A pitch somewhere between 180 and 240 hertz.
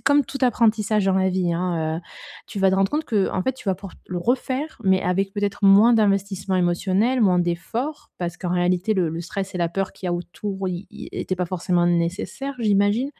Yes: high, 190 Hz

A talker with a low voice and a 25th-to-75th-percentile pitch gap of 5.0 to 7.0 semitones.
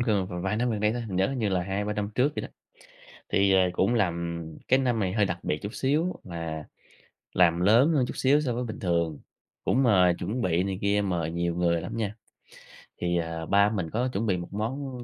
Yes: low, 100 Hz; average, 5.3 semitones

